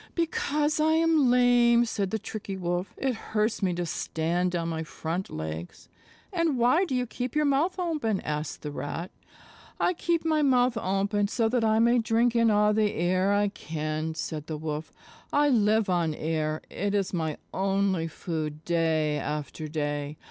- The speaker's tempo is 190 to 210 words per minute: No, average, 175 wpm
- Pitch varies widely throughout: Yes, wide, 7.3 semitones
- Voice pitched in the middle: No, high, 200 Hz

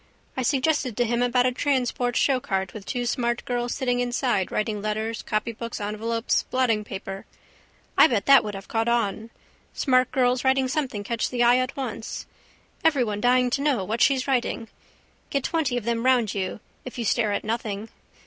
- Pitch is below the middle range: No, high, 240 Hz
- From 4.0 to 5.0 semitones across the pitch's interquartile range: No, average, 2.8 semitones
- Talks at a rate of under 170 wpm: No, average, 175 wpm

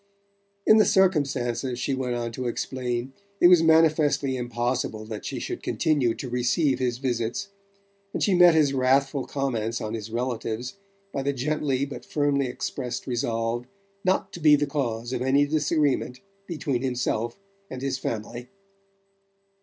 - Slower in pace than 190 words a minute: Yes, average, 150 wpm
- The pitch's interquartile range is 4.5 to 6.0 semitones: No, average, 3.3 semitones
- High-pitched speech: No, low, 130 Hz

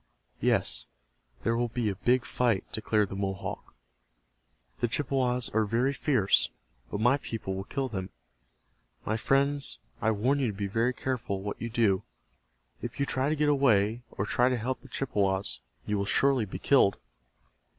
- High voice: No, low, 115 Hz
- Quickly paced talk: No, average, 170 wpm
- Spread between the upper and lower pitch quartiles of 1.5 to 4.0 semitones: No, average, 4.4 semitones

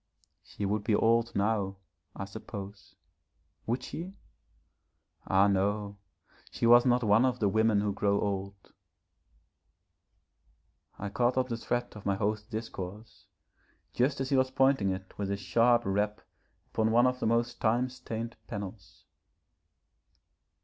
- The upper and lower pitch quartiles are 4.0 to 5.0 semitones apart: No, average, 3.2 semitones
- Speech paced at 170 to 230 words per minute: No, average, 140 wpm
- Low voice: Yes, low, 110 Hz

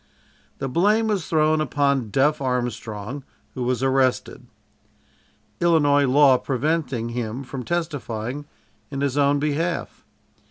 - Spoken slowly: Yes, slow, 115 wpm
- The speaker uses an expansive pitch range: No, average, 3.4 semitones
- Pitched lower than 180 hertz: Yes, medium, 140 Hz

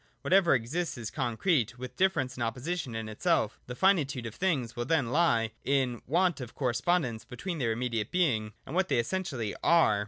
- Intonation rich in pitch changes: Yes, wide, 6.5 semitones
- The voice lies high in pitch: No, low, 130 Hz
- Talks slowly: No, average, 185 wpm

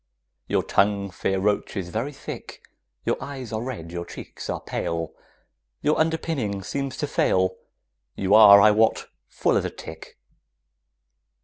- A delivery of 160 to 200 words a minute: No, average, 145 wpm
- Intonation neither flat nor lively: No, wide, 5.7 semitones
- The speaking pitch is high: No, low, 105 Hz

